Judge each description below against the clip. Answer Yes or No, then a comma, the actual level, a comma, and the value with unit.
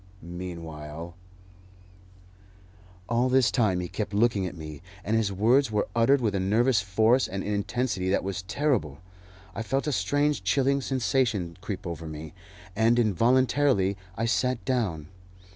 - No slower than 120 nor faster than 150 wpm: Yes, average, 145 wpm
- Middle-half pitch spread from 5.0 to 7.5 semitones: Yes, average, 5.3 semitones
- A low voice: Yes, low, 105 Hz